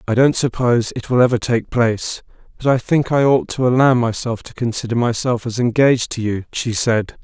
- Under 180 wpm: No, fast, 205 wpm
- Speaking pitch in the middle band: No, low, 120 Hz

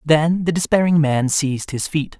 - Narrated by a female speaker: No, male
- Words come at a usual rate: Yes, average, 190 wpm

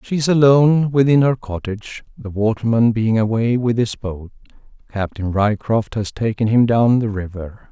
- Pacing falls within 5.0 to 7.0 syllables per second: No, 4.8 syllables/s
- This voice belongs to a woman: No, male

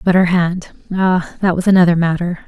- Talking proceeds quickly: No, average, 170 wpm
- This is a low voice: No, medium, 180 Hz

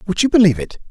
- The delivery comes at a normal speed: No, fast, 265 wpm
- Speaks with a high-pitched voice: No, medium, 180 Hz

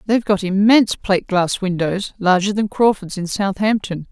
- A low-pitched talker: No, high, 195 Hz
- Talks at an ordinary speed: Yes, average, 160 wpm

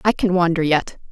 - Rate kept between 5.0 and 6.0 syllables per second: Yes, 5.4 syllables/s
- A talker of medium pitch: Yes, medium, 175 Hz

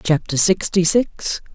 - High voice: No, medium, 170 Hz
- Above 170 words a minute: No, slow, 115 wpm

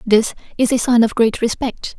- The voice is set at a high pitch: Yes, high, 235 Hz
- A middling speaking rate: No, fast, 210 wpm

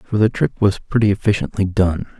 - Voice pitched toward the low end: Yes, low, 100 Hz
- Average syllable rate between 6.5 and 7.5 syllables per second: No, 5.5 syllables/s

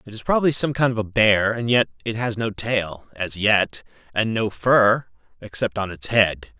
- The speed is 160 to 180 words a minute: No, average, 190 wpm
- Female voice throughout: No, male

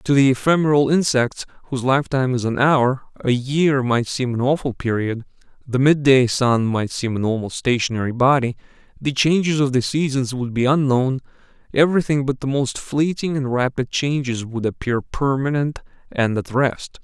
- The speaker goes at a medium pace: Yes, average, 170 wpm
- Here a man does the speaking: Yes, male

